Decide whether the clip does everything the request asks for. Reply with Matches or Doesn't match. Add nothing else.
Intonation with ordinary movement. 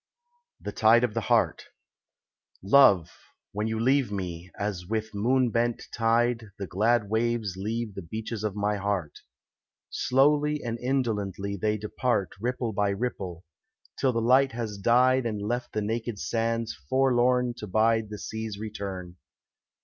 Matches